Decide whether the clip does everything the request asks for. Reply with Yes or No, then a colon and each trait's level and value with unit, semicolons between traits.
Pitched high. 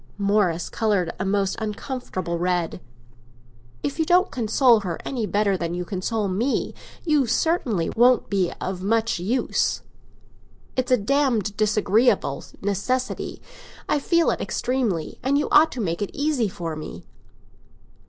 Yes: high, 215 Hz